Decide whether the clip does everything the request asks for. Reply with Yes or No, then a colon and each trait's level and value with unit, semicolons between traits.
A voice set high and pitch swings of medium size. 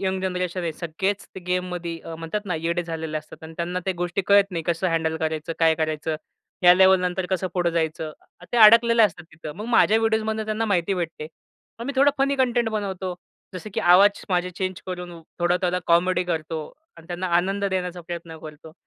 No: medium, 180 Hz; average, 3.0 semitones